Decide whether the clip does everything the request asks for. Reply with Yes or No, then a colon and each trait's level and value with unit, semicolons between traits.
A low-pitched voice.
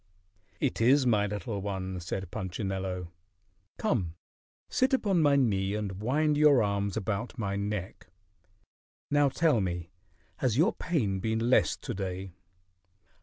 Yes: low, 105 Hz